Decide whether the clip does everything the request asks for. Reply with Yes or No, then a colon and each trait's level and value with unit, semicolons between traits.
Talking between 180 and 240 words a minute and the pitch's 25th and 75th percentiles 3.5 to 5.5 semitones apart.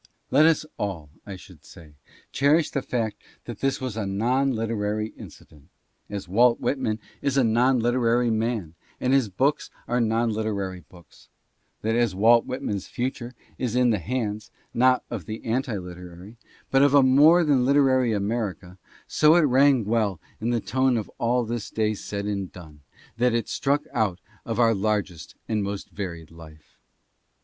No: average, 170 wpm; average, 4.2 semitones